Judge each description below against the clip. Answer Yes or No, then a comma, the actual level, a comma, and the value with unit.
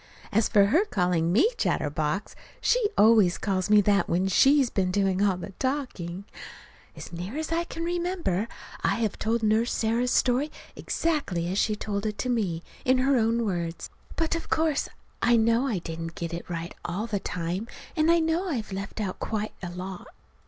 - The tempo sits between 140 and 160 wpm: No, average, 185 wpm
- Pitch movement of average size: No, wide, 6.1 semitones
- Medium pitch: No, high, 215 Hz